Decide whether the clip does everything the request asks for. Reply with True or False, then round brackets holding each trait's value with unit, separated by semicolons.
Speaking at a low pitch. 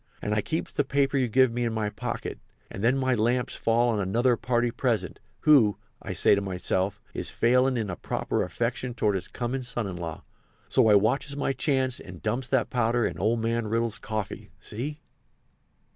True (120 Hz)